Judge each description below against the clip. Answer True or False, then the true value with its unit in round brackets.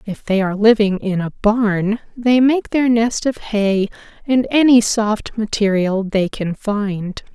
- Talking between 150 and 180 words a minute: True (165 wpm)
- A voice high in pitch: True (215 Hz)